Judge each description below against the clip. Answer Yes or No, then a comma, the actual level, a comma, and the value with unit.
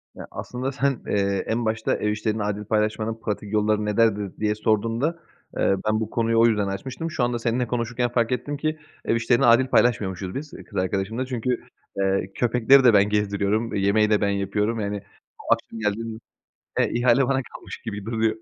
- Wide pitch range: No, average, 2.7 semitones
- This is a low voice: Yes, low, 110 Hz